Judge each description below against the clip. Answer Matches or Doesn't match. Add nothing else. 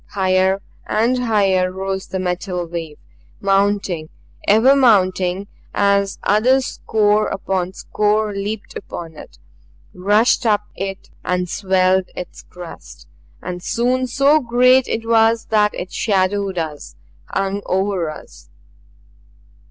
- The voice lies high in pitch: Matches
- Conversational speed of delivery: Doesn't match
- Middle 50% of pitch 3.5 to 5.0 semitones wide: Doesn't match